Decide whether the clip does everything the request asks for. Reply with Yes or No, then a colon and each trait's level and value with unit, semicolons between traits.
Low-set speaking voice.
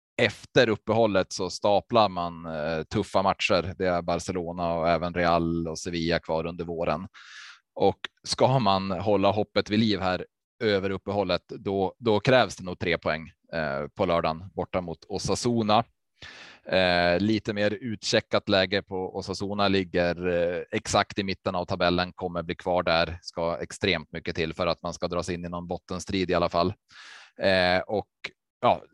Yes: very low, 90 Hz